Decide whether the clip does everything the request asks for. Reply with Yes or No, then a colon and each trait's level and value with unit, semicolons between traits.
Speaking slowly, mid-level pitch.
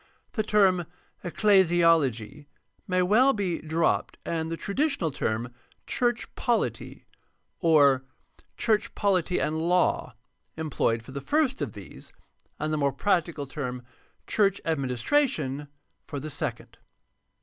Yes: slow, 130 wpm; medium, 165 Hz